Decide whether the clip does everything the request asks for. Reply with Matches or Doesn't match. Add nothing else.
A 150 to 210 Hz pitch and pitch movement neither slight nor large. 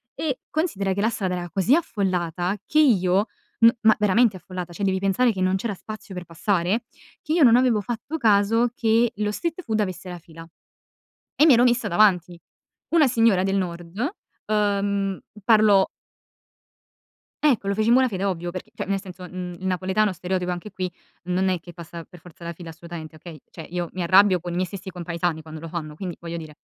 Matches